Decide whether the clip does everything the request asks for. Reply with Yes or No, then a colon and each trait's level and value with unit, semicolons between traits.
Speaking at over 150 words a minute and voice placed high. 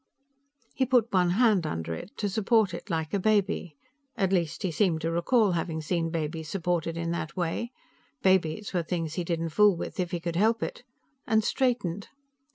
No: average, 185 wpm; medium, 175 Hz